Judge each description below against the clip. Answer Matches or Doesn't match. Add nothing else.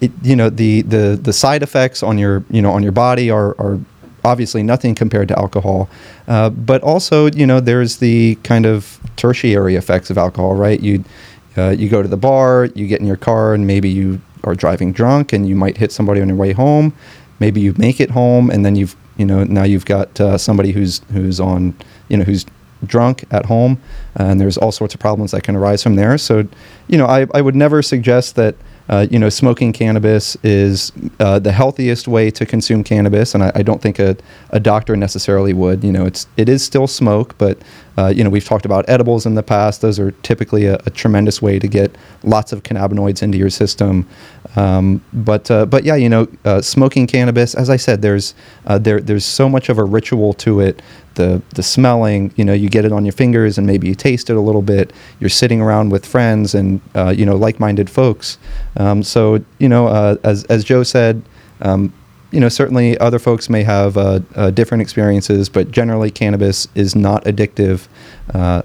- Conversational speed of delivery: Doesn't match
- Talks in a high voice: Doesn't match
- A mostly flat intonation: Doesn't match